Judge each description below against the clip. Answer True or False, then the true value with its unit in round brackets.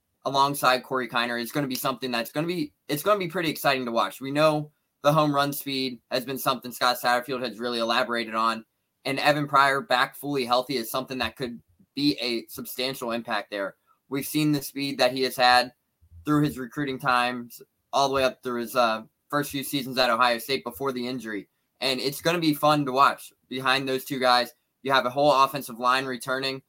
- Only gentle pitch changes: True (2.3 semitones)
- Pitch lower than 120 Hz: False (130 Hz)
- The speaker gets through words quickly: True (220 wpm)